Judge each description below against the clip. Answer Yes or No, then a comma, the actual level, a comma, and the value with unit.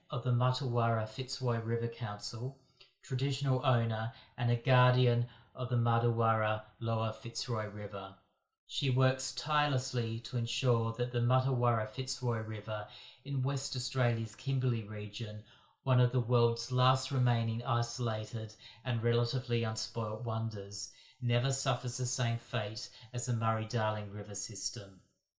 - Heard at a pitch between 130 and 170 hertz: No, low, 120 Hz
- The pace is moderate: No, slow, 130 wpm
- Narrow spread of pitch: Yes, narrow, 2.3 semitones